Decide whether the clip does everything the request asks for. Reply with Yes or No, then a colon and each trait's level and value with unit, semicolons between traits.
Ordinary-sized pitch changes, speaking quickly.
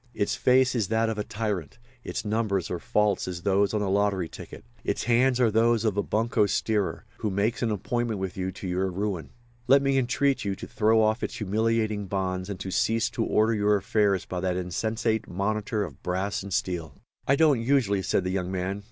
Yes: average, 3.0 semitones; fast, 210 wpm